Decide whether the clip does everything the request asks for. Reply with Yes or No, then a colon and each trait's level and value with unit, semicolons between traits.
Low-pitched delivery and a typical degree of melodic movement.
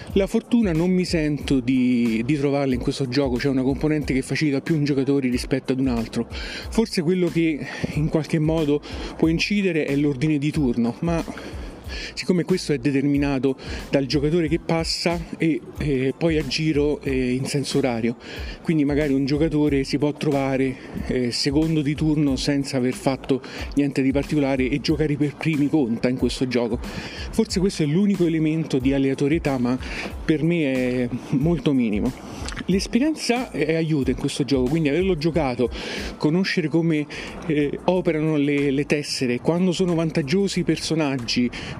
No: medium, 145 Hz; average, 3.3 semitones